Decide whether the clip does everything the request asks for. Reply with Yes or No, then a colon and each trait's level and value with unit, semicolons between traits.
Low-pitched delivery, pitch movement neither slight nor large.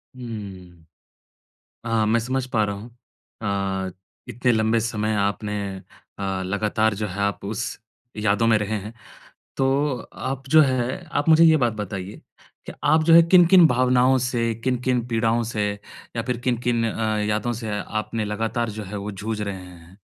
Yes: low, 110 Hz; average, 3.2 semitones